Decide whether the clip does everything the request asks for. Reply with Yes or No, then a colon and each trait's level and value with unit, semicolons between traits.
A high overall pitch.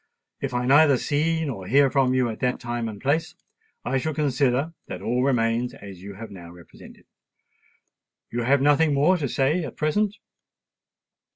No: low, 135 Hz